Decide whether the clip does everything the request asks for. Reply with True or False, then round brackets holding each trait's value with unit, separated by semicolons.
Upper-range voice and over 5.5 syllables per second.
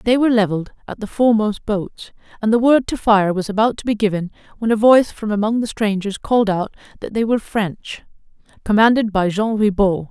True (215 Hz; 5.8 syllables/s)